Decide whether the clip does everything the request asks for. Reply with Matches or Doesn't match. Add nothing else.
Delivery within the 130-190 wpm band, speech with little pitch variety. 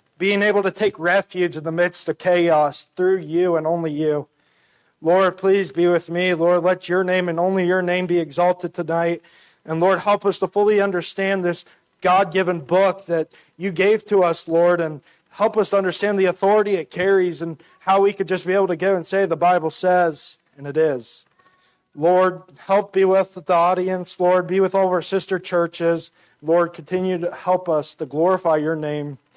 Doesn't match